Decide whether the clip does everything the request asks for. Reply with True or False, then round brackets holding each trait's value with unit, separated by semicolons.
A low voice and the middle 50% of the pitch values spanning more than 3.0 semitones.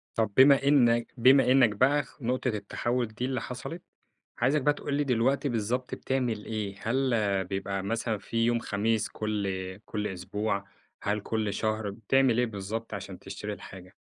True (115 Hz; 3.6 semitones)